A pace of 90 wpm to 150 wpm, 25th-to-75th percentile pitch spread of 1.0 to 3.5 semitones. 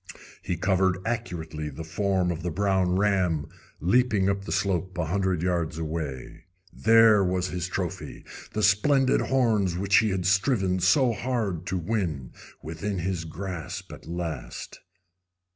Yes: average, 145 wpm; average, 3.1 semitones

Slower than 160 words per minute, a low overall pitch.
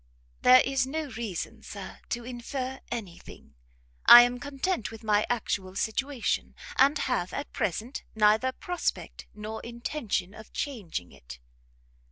No: slow, 135 wpm; high, 235 Hz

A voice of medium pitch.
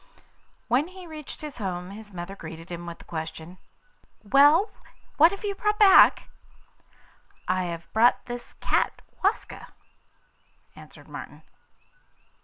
No: high, 220 Hz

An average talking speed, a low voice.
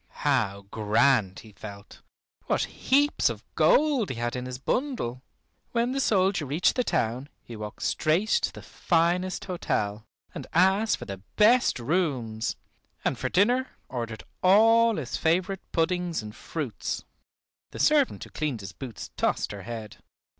No: average, 150 wpm; medium, 155 Hz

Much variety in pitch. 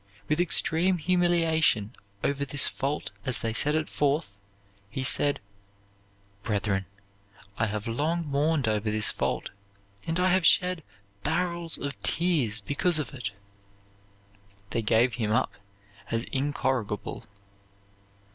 Yes: wide, 6.4 semitones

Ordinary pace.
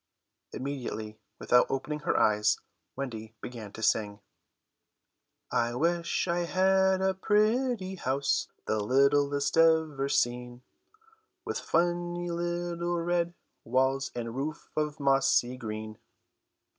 No: slow, 105 wpm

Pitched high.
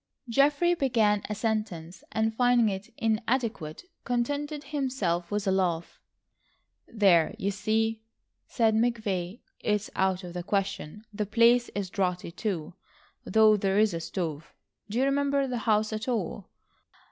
Yes: high, 215 Hz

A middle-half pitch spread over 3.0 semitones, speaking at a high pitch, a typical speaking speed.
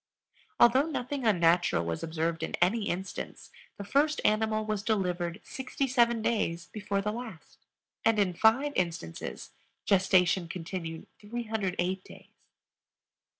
No: average, 4.6 semitones; high, 200 Hz; slow, 115 wpm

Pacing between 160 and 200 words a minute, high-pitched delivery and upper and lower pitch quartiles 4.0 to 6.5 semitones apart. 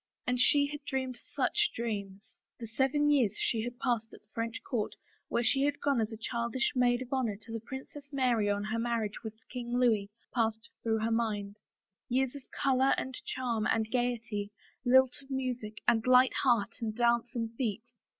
No: average, 190 wpm; high, 235 Hz; average, 2.7 semitones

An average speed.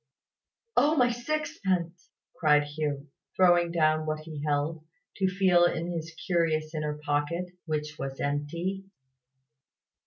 No: slow, 120 wpm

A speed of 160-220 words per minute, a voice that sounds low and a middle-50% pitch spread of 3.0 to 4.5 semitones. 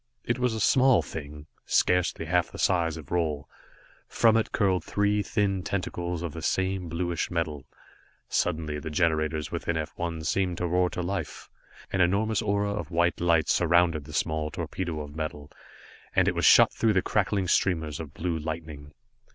Yes: average, 175 wpm; very low, 85 Hz; average, 3.3 semitones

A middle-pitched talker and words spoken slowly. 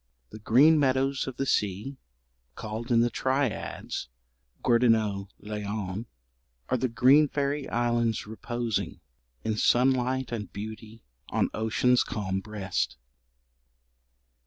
No: low, 115 Hz; slow, 110 wpm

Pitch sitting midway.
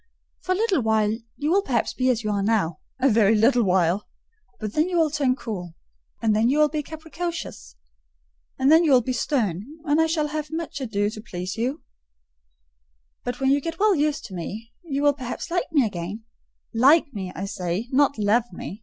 No: high, 245 Hz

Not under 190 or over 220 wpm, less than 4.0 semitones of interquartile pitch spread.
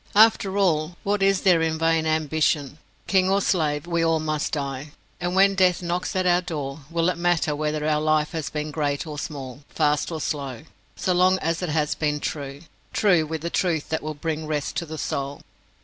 Yes: fast, 205 wpm; average, 2.9 semitones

